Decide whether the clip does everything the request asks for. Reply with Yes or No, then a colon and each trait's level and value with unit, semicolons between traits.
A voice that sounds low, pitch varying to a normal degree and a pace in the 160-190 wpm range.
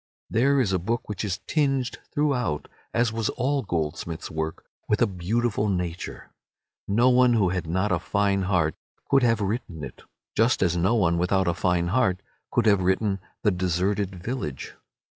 Yes: low, 100 Hz; average, 4.9 semitones; average, 170 wpm